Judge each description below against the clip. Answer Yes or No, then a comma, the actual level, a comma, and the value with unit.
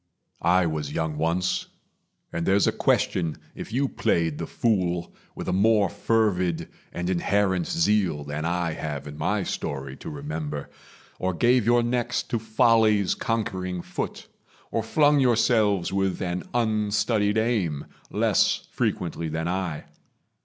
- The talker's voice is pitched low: Yes, very low, 95 Hz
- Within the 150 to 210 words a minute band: No, average, 140 wpm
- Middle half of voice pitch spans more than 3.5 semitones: Yes, average, 5.2 semitones